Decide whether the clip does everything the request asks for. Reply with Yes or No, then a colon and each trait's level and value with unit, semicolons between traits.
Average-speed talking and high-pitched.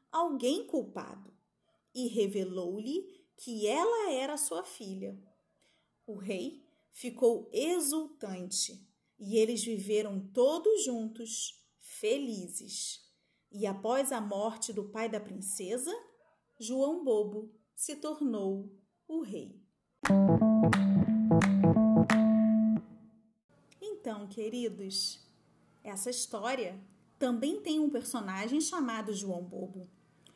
No: slow, 85 wpm; high, 220 Hz